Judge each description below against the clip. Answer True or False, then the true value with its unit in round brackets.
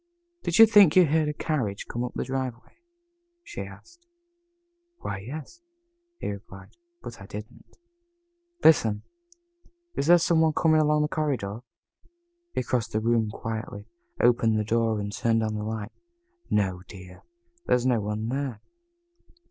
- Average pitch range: False (6.2 semitones)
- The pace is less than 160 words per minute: True (150 wpm)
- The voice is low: True (115 Hz)